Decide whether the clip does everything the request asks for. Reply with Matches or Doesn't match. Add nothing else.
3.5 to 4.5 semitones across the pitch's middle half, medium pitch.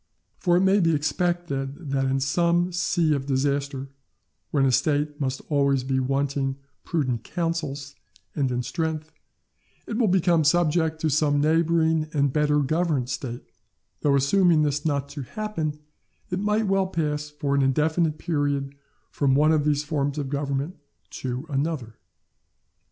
Doesn't match